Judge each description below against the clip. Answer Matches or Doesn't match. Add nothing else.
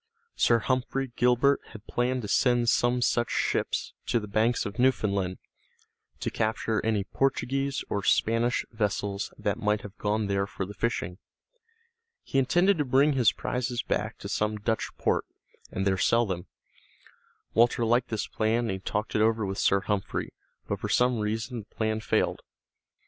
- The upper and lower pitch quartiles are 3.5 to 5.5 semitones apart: Doesn't match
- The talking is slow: Doesn't match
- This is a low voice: Matches